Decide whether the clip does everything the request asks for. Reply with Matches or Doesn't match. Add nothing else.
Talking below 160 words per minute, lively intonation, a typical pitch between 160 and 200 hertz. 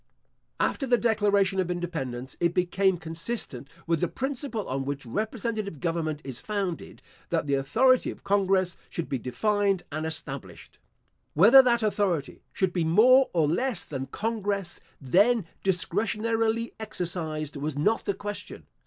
Matches